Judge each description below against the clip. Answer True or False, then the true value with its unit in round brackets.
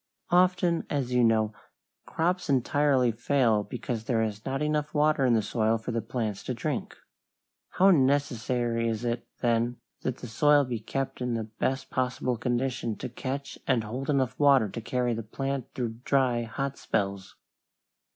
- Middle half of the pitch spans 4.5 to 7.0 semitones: False (3.3 semitones)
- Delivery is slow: False (165 wpm)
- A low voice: True (125 Hz)